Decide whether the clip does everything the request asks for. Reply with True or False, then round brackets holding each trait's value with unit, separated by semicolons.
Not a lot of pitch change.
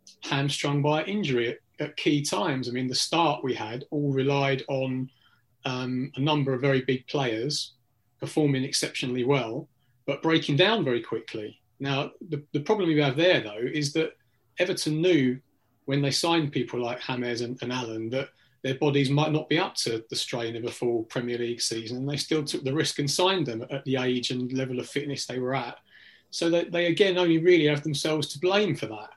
False (3.4 semitones)